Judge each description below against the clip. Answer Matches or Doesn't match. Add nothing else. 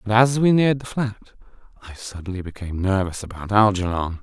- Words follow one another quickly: Doesn't match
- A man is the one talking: Matches